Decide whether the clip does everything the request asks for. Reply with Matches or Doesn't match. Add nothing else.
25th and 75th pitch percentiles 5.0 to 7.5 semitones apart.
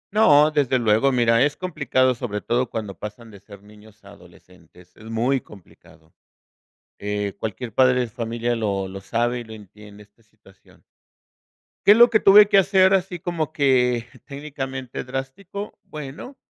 Matches